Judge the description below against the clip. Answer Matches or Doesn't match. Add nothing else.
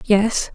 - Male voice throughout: Doesn't match